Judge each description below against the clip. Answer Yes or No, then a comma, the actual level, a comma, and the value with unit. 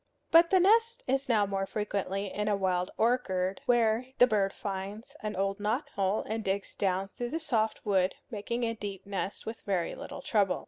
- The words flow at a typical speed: Yes, average, 190 wpm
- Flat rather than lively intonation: No, average, 3.5 semitones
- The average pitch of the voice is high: Yes, high, 210 Hz